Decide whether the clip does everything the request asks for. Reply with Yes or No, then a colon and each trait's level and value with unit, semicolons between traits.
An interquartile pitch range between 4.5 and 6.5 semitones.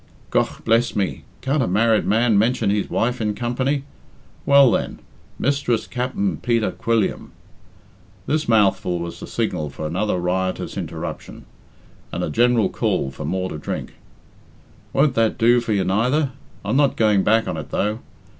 No: average, 4.1 semitones